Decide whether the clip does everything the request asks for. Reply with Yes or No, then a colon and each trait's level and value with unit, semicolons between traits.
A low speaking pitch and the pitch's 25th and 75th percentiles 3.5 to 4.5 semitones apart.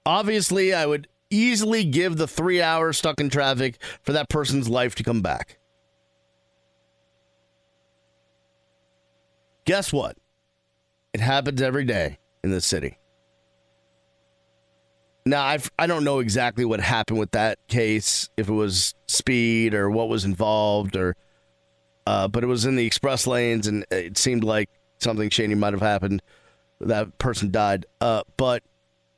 No: low, 115 Hz; average, 2.7 semitones